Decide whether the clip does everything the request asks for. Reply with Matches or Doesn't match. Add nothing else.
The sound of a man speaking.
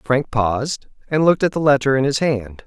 Matches